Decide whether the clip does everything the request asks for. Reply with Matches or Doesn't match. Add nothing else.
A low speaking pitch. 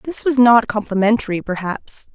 Doesn't match